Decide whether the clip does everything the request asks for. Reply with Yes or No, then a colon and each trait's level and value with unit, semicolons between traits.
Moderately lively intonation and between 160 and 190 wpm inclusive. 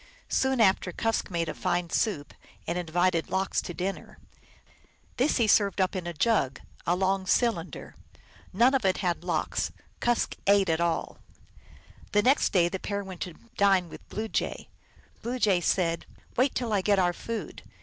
Yes: average, 3.8 semitones; average, 175 wpm